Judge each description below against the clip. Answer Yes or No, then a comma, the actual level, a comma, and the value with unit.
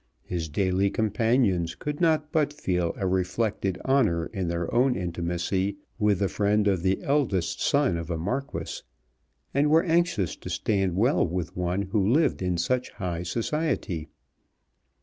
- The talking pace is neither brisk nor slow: Yes, average, 150 wpm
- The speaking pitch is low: Yes, low, 100 Hz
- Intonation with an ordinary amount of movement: No, wide, 6.2 semitones